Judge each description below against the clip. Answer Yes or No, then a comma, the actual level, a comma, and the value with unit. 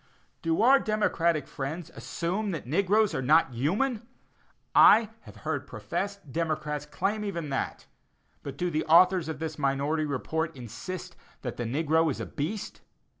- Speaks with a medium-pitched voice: Yes, medium, 160 Hz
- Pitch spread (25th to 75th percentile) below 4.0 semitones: No, average, 5.0 semitones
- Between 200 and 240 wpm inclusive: No, average, 155 wpm